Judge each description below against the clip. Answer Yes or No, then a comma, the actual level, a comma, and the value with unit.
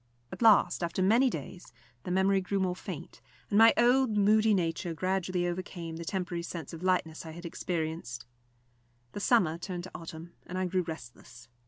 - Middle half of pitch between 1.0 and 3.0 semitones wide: Yes, narrow, 2.6 semitones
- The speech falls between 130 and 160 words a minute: No, average, 175 wpm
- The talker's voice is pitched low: No, medium, 180 Hz